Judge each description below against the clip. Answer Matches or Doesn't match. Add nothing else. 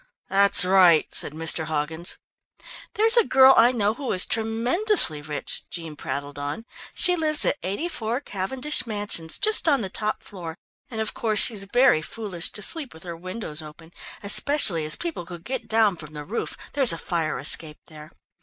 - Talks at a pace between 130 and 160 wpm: Doesn't match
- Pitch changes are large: Matches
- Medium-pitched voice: Doesn't match